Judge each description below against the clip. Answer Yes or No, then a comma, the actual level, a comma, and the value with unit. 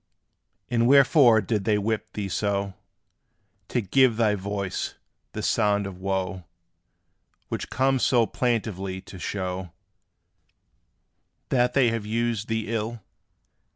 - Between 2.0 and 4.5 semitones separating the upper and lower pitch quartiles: Yes, average, 3.2 semitones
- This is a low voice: Yes, low, 110 Hz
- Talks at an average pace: No, slow, 120 wpm